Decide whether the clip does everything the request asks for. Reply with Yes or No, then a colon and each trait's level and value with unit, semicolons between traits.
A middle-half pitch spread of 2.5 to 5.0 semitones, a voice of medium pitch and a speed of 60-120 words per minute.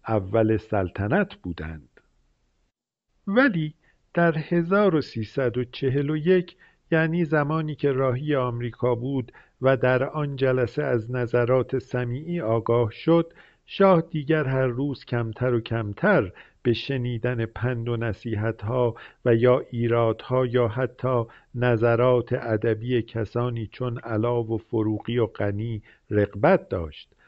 No: average, 3.2 semitones; low, 125 Hz; average, 110 wpm